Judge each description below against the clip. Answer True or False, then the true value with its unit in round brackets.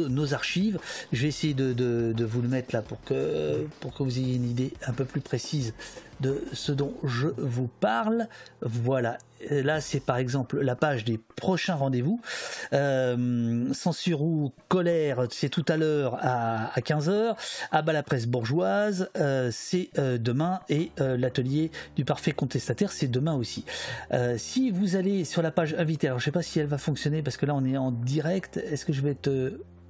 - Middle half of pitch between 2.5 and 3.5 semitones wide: False (4.1 semitones)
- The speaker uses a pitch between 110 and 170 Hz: True (140 Hz)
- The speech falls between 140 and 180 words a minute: False (205 wpm)